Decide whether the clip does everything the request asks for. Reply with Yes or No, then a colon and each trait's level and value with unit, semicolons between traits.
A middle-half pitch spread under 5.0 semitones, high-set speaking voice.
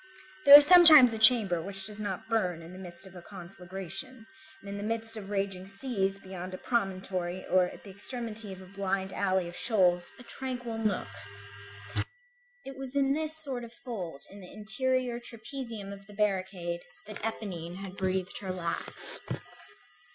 Yes: average, 3.9 semitones; high, 200 Hz